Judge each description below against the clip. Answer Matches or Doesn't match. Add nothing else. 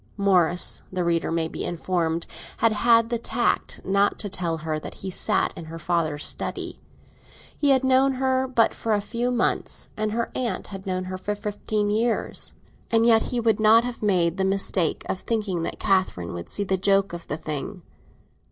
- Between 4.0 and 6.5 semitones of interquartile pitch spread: Matches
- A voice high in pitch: Matches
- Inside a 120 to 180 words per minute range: Doesn't match